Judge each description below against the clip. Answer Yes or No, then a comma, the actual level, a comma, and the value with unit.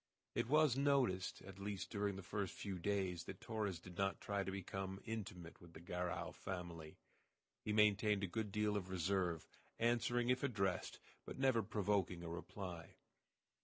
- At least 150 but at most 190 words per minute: Yes, average, 165 wpm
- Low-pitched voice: Yes, very low, 95 Hz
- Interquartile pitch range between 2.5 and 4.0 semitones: Yes, average, 2.9 semitones